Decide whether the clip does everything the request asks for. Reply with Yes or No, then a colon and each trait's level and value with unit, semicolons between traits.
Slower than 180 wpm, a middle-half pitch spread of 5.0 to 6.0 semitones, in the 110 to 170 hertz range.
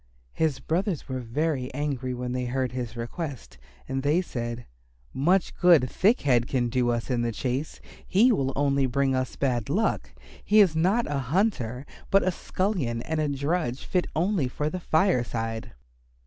Yes: average, 170 wpm; wide, 5.5 semitones; medium, 140 Hz